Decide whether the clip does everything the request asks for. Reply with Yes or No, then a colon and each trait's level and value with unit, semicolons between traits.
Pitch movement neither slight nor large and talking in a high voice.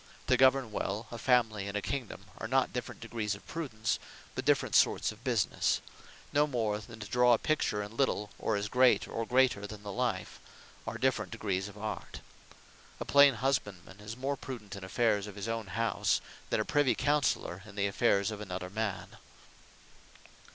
No: average, 3.6 semitones; low, 110 Hz